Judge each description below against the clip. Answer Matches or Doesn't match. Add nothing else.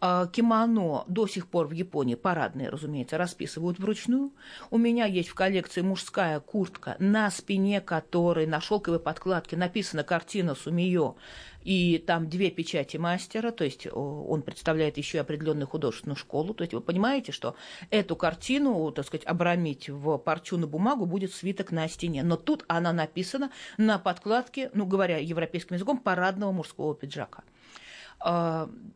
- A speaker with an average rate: Matches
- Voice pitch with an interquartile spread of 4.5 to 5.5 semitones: Doesn't match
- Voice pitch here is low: Doesn't match